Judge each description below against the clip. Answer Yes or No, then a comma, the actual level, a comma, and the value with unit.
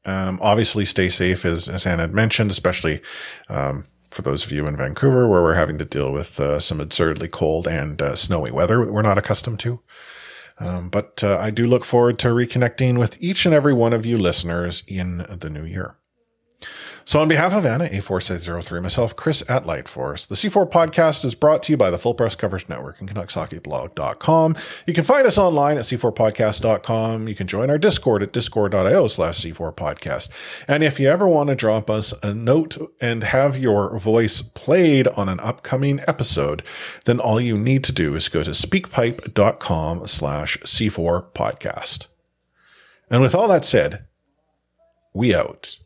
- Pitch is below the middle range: Yes, low, 110 Hz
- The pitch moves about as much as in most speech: No, wide, 6.9 semitones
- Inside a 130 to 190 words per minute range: Yes, average, 180 wpm